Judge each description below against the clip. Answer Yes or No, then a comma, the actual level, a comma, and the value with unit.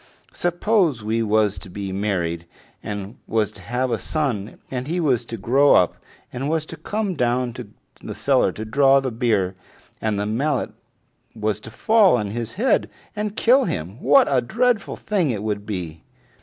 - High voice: No, low, 120 Hz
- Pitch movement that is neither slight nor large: No, wide, 6.3 semitones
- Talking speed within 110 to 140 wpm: No, average, 180 wpm